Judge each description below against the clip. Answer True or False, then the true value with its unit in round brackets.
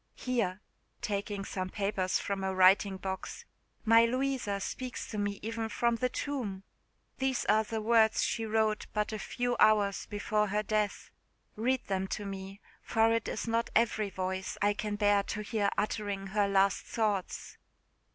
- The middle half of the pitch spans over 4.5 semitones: False (2.4 semitones)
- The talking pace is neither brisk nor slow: True (160 wpm)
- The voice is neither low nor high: False (210 Hz)